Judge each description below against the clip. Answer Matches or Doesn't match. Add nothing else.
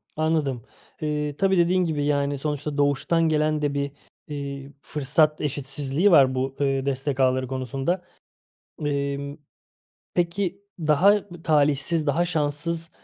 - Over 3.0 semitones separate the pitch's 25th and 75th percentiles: Doesn't match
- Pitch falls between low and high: Matches